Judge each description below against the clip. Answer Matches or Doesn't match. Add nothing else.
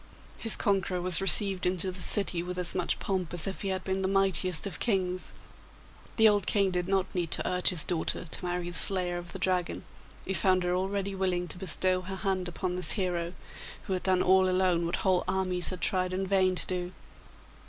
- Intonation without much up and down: Matches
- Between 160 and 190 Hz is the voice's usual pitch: Matches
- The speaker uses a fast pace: Matches